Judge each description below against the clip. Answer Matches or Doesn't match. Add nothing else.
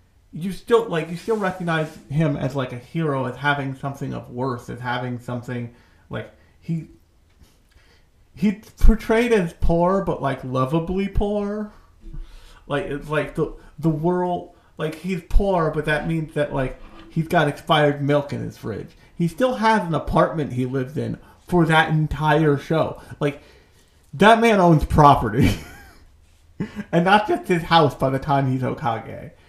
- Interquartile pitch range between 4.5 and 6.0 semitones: Matches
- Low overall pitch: Doesn't match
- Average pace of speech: Matches